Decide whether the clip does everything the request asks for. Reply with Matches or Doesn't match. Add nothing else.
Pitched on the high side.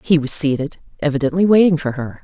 Doesn't match